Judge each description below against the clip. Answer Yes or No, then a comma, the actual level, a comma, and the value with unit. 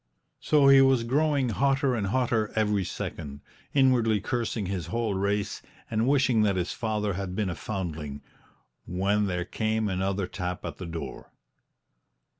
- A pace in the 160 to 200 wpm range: No, average, 150 wpm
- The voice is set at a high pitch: No, low, 105 Hz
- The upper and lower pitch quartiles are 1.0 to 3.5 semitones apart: No, average, 4.5 semitones